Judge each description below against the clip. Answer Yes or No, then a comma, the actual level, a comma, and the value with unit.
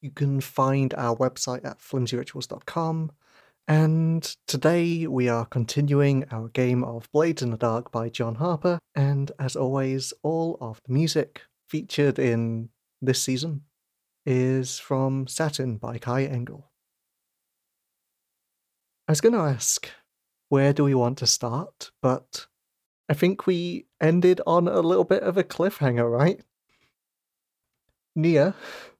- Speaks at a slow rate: Yes, slow, 130 wpm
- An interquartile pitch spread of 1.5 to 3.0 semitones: No, average, 4.5 semitones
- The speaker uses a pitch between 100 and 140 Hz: Yes, low, 135 Hz